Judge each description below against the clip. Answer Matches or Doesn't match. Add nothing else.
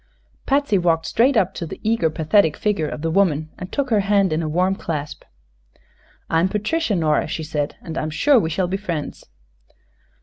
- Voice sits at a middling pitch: Matches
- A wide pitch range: Doesn't match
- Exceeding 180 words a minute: Matches